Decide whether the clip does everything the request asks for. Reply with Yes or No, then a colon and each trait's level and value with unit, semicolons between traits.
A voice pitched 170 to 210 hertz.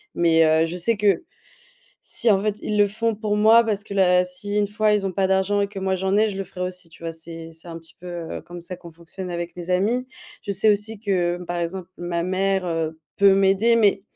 Yes: high, 190 Hz